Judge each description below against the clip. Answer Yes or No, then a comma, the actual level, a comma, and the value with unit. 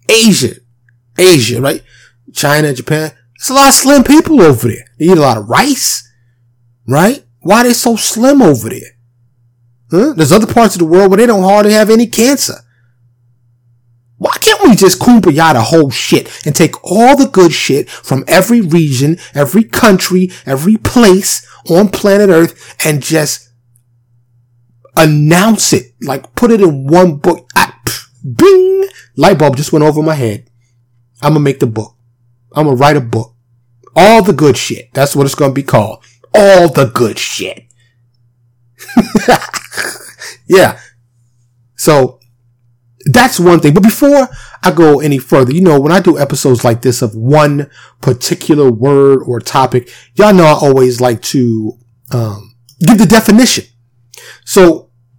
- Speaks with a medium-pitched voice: Yes, medium, 145 Hz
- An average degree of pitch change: No, wide, 7.8 semitones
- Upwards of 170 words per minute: No, average, 155 wpm